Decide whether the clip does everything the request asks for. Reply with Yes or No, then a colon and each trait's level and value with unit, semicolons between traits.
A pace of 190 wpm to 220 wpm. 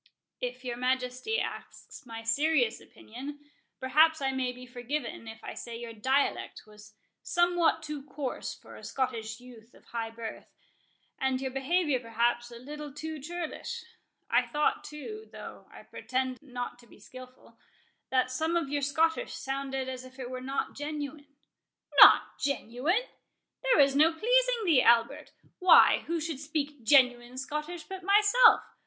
No: average, 145 wpm